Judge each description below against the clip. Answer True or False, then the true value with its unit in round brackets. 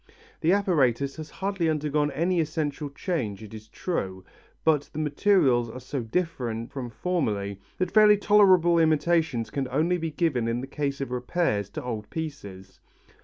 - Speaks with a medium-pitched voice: True (145 Hz)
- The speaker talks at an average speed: True (160 wpm)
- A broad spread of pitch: True (6.0 semitones)